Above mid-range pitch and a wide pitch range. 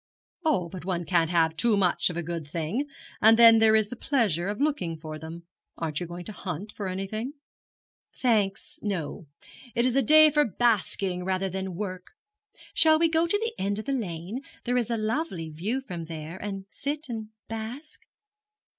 Yes: high, 205 Hz; wide, 5.9 semitones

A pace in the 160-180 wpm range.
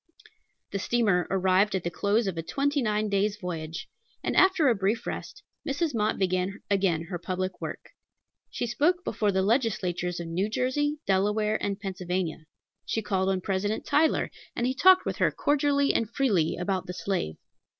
Yes: average, 170 wpm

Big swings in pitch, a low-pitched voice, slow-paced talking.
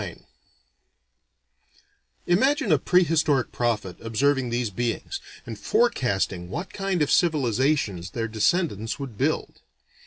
Yes: wide, 7.2 semitones; low, 130 Hz; slow, 105 wpm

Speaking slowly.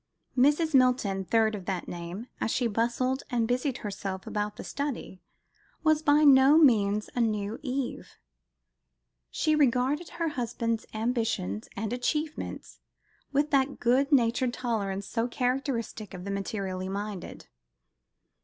Yes: slow, 130 wpm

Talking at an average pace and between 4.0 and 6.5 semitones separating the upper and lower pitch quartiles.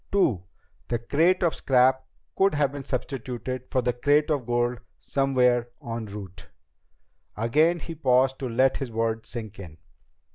No: average, 150 wpm; average, 3.3 semitones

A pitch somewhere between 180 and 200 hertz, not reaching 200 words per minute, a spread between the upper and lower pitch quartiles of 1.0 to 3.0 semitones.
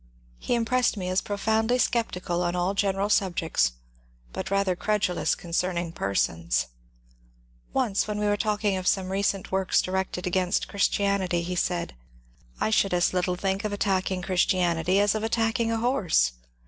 Yes: high, 190 Hz; average, 165 wpm; average, 2.7 semitones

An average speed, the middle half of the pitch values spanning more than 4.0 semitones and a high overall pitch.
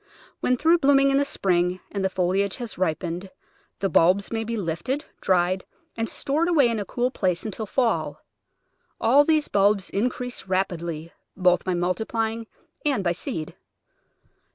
Yes: average, 155 wpm; wide, 5.5 semitones; high, 200 Hz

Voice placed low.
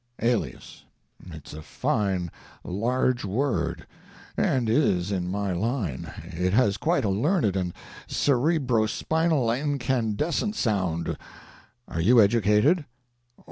Yes: low, 110 Hz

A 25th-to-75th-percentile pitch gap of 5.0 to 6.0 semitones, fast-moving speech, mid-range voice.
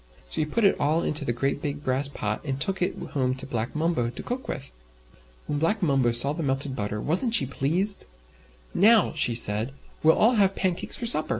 Yes: wide, 5.5 semitones; fast, 210 wpm; medium, 145 Hz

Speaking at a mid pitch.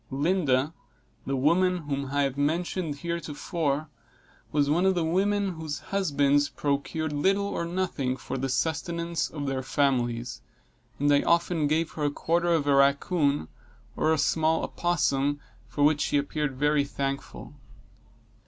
Yes: medium, 150 Hz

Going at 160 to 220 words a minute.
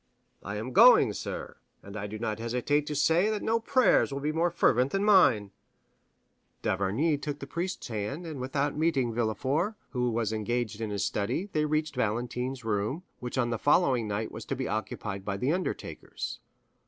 Yes: average, 180 wpm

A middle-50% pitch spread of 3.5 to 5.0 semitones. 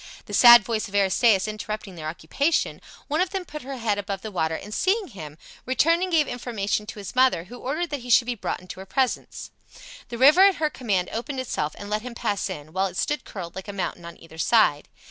No: wide, 5.6 semitones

